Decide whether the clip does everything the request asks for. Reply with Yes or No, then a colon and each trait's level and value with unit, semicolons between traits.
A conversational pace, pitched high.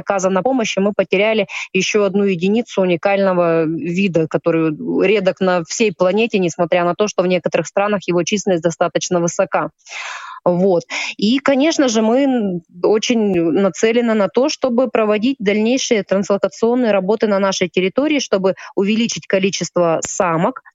Yes: average, 135 wpm; high, 195 Hz